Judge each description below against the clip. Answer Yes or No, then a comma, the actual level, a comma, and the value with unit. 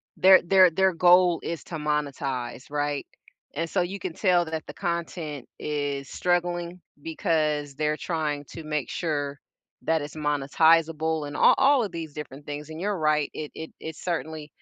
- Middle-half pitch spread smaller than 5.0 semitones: Yes, average, 2.8 semitones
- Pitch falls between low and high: Yes, medium, 160 Hz